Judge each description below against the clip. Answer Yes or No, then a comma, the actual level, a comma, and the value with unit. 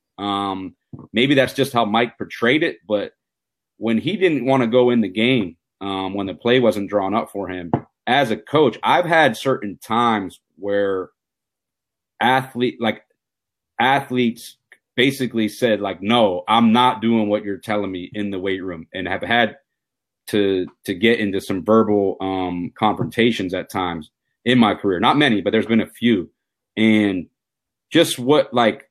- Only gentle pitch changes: No, average, 3.6 semitones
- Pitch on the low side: Yes, low, 110 Hz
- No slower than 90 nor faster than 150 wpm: No, average, 165 wpm